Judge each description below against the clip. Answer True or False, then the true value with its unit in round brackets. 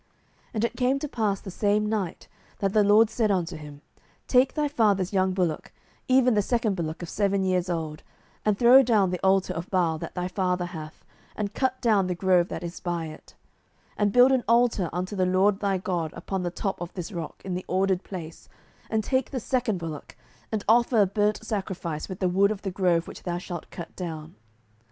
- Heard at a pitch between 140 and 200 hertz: True (190 Hz)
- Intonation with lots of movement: False (3.4 semitones)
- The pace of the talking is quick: True (215 wpm)